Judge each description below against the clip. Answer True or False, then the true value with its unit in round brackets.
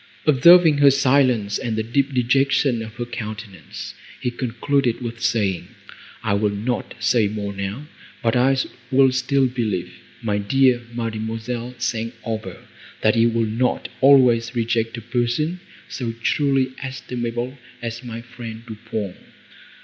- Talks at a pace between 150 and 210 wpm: False (140 wpm)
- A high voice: False (120 Hz)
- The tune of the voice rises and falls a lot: False (2.6 semitones)